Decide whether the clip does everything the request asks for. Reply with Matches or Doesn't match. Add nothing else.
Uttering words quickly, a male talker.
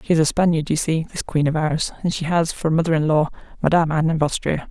Doesn't match